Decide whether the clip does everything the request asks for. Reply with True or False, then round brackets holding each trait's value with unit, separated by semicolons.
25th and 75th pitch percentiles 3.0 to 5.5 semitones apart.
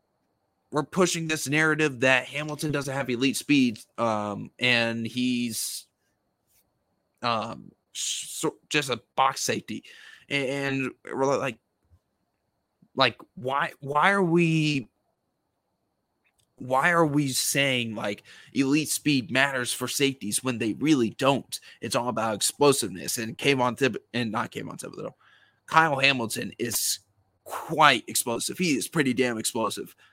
True (3.8 semitones)